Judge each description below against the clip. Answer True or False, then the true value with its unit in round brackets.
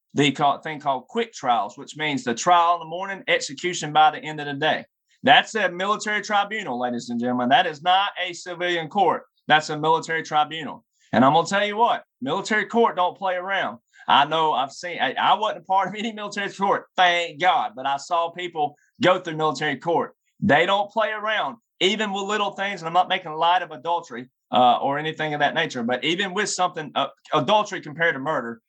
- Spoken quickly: True (210 wpm)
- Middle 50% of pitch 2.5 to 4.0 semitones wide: False (4.6 semitones)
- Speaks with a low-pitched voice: False (175 Hz)